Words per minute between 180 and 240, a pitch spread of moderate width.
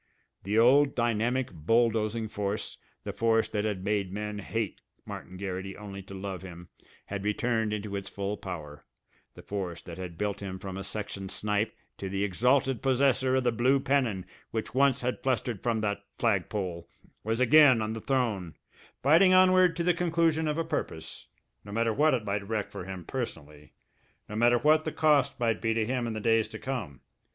Yes: average, 185 wpm; average, 4.5 semitones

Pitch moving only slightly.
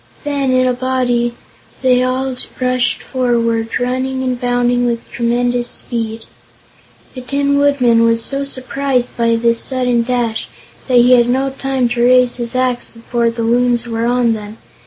Yes: narrow, 1.4 semitones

